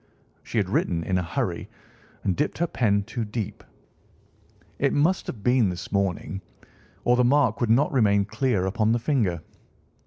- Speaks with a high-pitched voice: No, low, 110 Hz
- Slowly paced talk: No, average, 165 wpm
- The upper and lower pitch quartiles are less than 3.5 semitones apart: No, average, 4.3 semitones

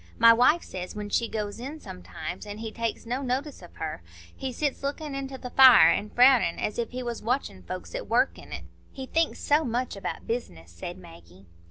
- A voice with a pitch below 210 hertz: No, high, 230 Hz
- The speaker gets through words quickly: Yes, fast, 210 wpm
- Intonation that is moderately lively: No, wide, 6.3 semitones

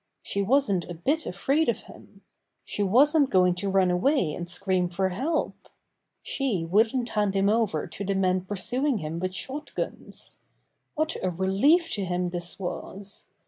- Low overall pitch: No, high, 195 Hz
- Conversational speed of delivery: Yes, average, 165 wpm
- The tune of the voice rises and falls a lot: Yes, wide, 6.3 semitones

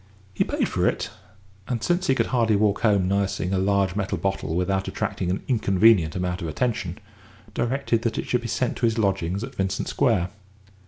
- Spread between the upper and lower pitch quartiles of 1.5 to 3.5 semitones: No, average, 3.9 semitones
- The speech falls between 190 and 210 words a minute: Yes, average, 195 wpm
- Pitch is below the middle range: Yes, low, 100 Hz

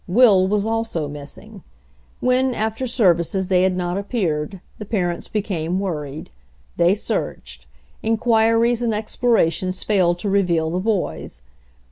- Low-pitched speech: No, high, 195 Hz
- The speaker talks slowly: Yes, slow, 125 wpm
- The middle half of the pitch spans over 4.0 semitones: Yes, average, 4.4 semitones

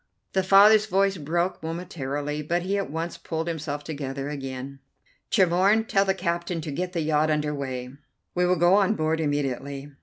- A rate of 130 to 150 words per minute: No, average, 175 wpm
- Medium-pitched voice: Yes, medium, 160 Hz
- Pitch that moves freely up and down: No, average, 4.0 semitones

